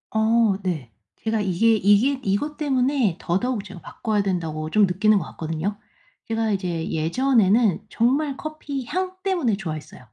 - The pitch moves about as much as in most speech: No, wide, 5.9 semitones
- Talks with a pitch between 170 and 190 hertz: No, high, 215 Hz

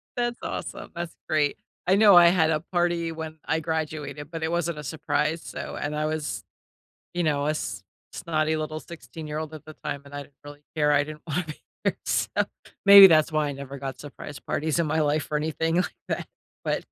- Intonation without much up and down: Yes, narrow, 2.0 semitones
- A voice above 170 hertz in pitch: No, medium, 155 Hz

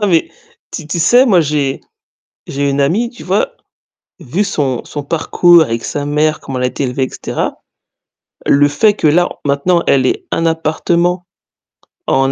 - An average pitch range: Yes, average, 4.0 semitones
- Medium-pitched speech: Yes, medium, 155 Hz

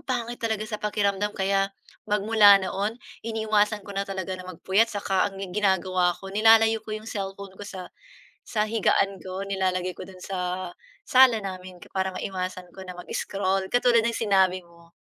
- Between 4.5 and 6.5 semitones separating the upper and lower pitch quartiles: No, narrow, 2.5 semitones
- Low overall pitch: No, high, 195 Hz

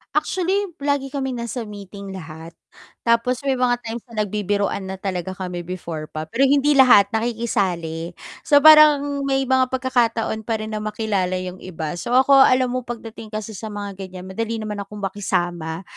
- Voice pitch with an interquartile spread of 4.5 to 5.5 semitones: Yes, average, 5.2 semitones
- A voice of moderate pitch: No, high, 215 Hz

